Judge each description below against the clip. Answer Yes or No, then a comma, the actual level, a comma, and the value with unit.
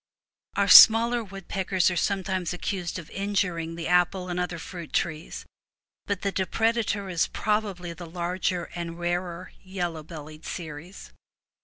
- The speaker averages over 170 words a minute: No, slow, 135 wpm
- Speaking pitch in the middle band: Yes, medium, 180 Hz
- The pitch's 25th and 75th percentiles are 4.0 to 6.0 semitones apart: No, narrow, 2.4 semitones